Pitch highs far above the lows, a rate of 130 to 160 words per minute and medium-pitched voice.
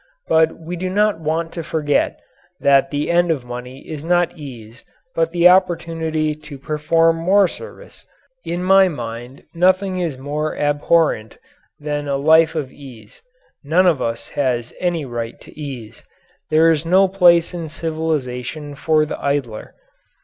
No: average, 3.3 semitones; average, 150 wpm; medium, 155 Hz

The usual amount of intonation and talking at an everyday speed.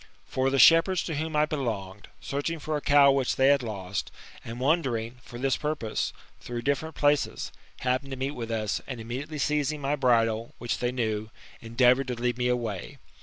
Yes: average, 3.7 semitones; average, 185 wpm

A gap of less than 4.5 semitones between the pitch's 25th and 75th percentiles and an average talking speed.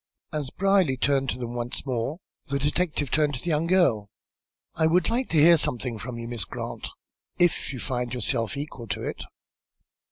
No: average, 4.8 semitones; average, 185 wpm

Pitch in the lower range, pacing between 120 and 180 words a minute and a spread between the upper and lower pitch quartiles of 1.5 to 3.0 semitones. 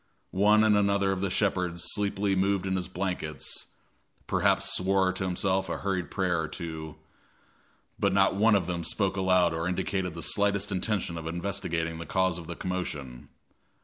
Yes: very low, 95 Hz; average, 170 wpm; narrow, 2.4 semitones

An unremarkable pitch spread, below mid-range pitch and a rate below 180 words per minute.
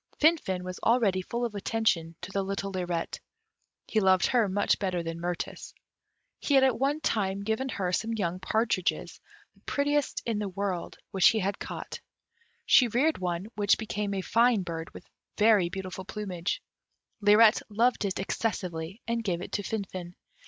No: average, 3.6 semitones; high, 200 Hz; average, 165 wpm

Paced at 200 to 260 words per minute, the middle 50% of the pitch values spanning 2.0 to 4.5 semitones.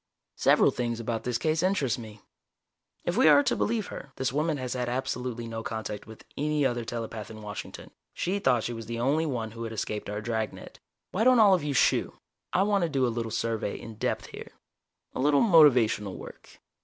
No: fast, 205 wpm; average, 5.2 semitones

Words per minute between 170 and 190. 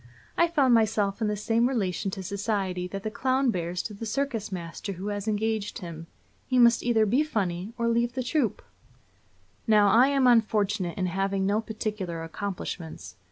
Yes: average, 175 wpm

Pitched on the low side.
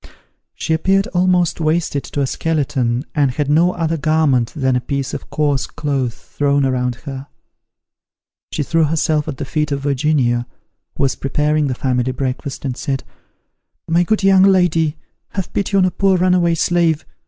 No: medium, 150 Hz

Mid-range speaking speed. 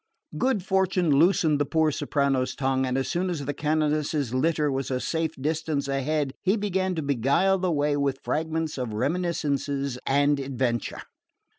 Yes: average, 160 wpm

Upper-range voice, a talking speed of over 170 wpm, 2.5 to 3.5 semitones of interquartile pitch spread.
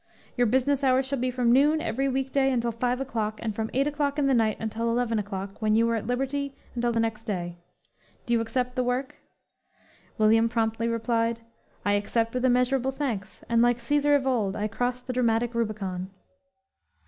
Yes: high, 240 Hz; average, 195 wpm; average, 2.8 semitones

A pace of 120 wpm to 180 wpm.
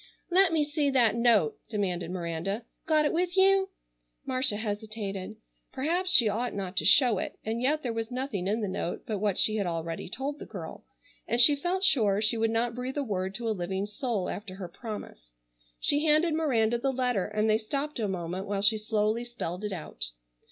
No: average, 200 wpm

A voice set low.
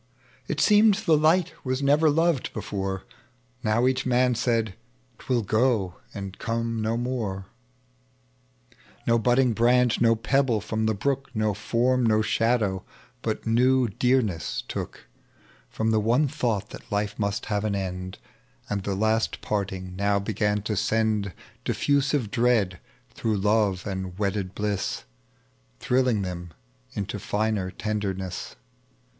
Yes: low, 110 Hz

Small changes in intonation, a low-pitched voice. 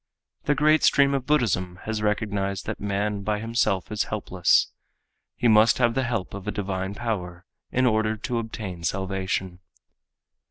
No: average, 3.5 semitones; low, 105 Hz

